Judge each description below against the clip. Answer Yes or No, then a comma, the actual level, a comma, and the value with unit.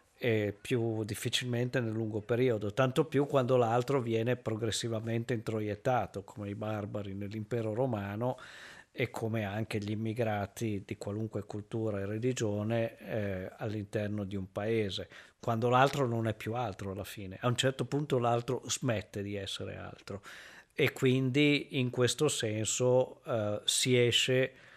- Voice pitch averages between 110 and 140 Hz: Yes, low, 115 Hz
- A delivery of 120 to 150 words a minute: Yes, average, 140 wpm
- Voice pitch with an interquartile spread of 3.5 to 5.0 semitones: No, average, 3.1 semitones